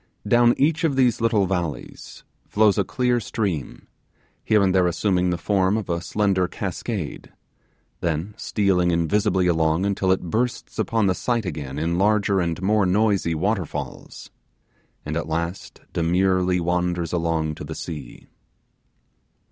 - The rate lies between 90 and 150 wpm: Yes, average, 140 wpm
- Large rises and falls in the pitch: No, average, 3.8 semitones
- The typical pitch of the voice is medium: No, very low, 95 Hz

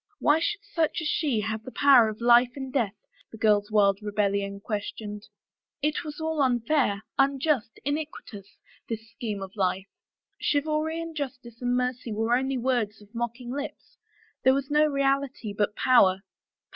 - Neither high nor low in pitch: No, high, 245 Hz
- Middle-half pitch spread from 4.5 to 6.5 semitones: Yes, average, 5.0 semitones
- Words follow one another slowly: No, average, 160 wpm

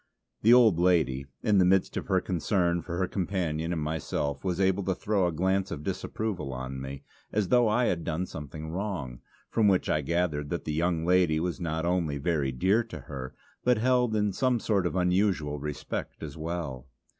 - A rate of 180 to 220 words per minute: Yes, average, 195 wpm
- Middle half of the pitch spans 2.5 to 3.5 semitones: No, average, 4.1 semitones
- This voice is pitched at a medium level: No, very low, 85 Hz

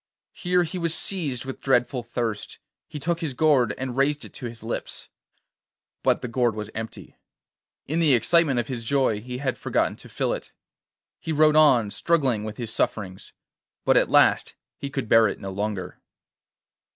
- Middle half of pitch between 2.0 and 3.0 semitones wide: No, average, 5.0 semitones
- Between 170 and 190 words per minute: Yes, average, 175 wpm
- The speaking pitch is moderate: No, low, 130 Hz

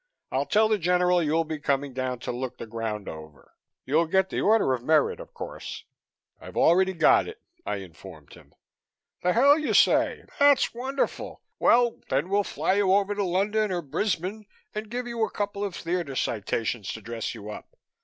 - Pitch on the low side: No, medium, 180 Hz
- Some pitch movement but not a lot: No, wide, 8.2 semitones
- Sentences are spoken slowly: No, average, 190 wpm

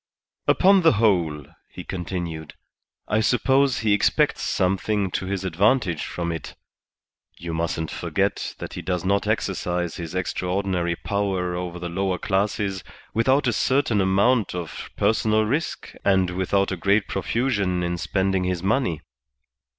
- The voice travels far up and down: No, average, 3.3 semitones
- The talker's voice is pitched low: Yes, very low, 95 Hz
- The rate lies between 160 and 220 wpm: No, average, 140 wpm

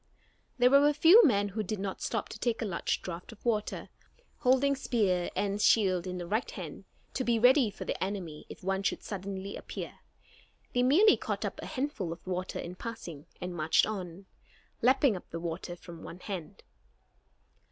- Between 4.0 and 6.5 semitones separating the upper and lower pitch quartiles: Yes, average, 5.3 semitones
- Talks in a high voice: Yes, high, 200 Hz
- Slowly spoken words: No, average, 190 wpm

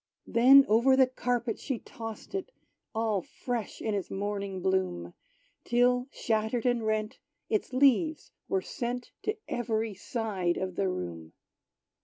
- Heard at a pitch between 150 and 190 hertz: No, high, 225 Hz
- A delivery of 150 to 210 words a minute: No, slow, 135 wpm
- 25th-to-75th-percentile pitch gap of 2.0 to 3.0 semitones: No, average, 3.9 semitones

